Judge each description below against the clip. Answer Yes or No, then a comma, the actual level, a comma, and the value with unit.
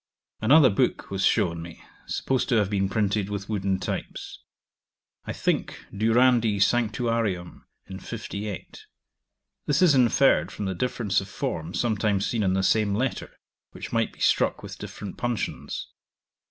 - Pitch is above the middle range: No, low, 105 Hz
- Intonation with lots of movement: No, average, 3.5 semitones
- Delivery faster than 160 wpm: No, average, 145 wpm